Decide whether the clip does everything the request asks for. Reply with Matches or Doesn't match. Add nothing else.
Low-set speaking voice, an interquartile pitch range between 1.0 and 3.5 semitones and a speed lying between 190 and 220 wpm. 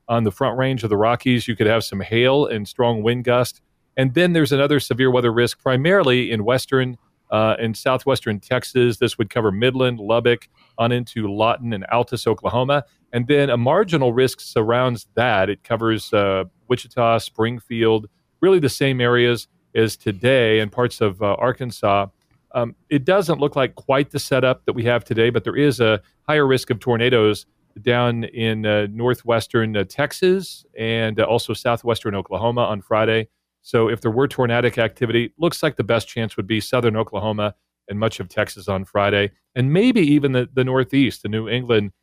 Doesn't match